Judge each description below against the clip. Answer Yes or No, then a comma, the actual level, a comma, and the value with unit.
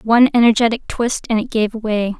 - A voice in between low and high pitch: No, high, 225 Hz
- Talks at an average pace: Yes, average, 190 wpm